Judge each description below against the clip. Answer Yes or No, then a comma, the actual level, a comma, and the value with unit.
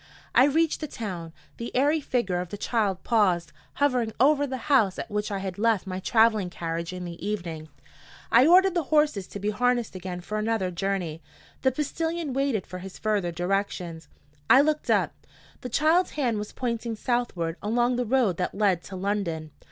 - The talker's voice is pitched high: Yes, high, 210 Hz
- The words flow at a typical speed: Yes, average, 185 wpm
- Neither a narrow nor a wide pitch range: No, wide, 5.9 semitones